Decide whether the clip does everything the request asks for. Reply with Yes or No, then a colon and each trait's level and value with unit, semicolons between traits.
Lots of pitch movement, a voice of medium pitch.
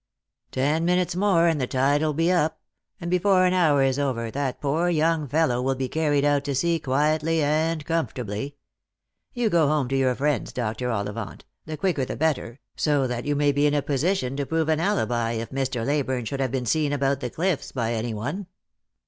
No: average, 3.8 semitones; medium, 145 Hz